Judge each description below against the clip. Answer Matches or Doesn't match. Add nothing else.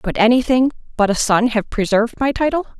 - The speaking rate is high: Matches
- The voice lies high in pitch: Matches